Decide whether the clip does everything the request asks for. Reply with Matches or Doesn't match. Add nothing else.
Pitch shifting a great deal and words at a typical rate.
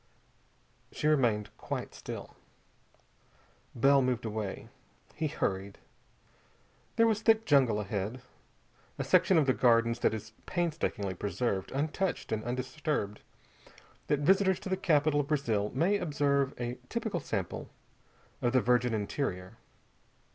Doesn't match